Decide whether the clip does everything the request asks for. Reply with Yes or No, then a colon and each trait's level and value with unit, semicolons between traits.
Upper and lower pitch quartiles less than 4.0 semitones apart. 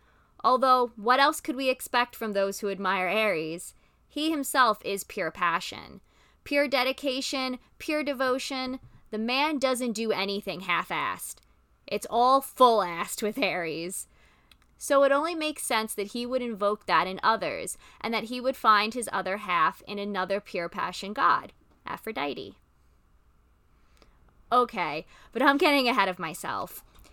No: average, 5.1 semitones